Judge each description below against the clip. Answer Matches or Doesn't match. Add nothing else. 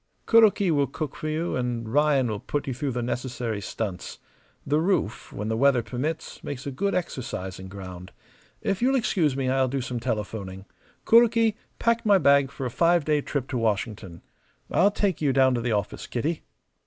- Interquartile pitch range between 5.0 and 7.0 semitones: Matches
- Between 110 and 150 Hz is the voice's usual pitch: Matches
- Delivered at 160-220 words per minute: Matches